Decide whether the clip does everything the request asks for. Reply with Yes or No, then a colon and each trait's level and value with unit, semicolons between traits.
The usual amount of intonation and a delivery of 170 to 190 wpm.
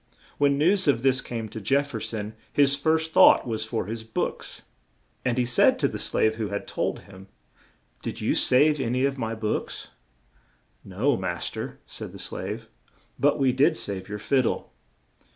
Yes: average, 4.3 semitones; average, 185 wpm